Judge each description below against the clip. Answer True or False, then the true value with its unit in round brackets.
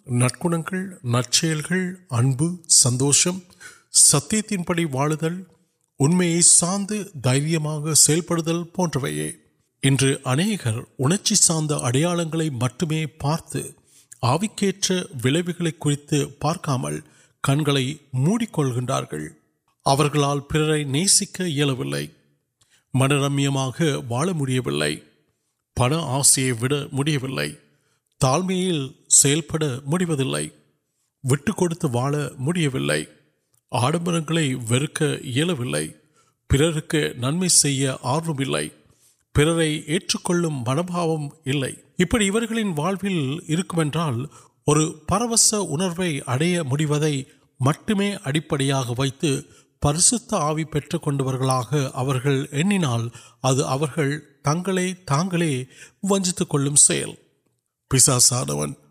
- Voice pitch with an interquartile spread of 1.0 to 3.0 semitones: False (4.2 semitones)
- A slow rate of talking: True (45 wpm)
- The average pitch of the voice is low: False (150 Hz)